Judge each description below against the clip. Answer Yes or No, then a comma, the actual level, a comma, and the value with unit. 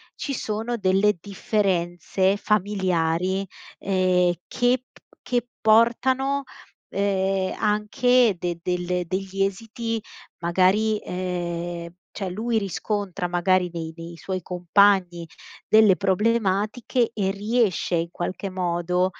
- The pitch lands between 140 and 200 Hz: Yes, high, 190 Hz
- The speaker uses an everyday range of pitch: Yes, average, 3.1 semitones